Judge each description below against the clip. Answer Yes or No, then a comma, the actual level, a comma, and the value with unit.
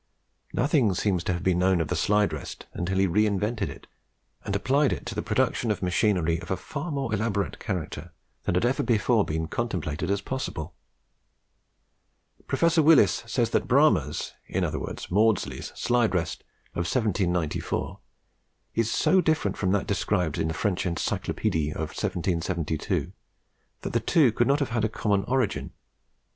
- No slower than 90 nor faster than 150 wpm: No, average, 165 wpm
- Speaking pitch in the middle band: No, low, 100 Hz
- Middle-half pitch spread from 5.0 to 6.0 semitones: Yes, average, 5.3 semitones